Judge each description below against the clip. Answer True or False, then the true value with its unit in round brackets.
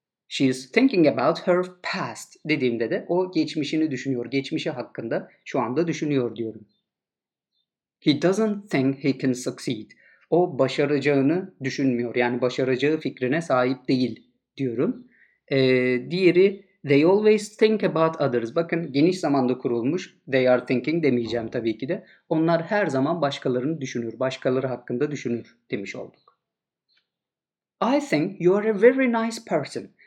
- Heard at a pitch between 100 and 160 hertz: True (140 Hz)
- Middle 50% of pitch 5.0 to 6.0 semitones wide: True (5.4 semitones)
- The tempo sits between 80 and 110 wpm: False (135 wpm)